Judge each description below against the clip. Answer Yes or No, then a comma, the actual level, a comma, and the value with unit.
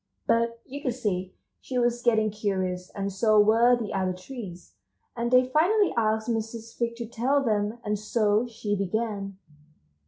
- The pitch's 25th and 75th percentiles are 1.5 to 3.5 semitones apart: Yes, average, 2.7 semitones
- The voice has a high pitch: Yes, high, 220 Hz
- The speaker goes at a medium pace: Yes, average, 160 wpm